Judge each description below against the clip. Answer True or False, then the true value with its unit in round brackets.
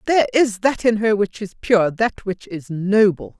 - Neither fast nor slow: False (210 wpm)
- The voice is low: False (210 Hz)